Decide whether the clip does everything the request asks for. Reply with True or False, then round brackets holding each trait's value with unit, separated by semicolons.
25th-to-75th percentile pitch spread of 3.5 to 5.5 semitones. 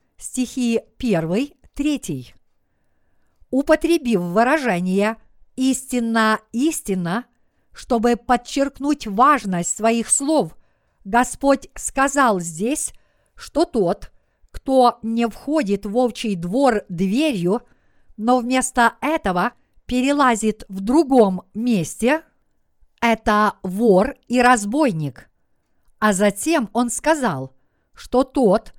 True (4.3 semitones)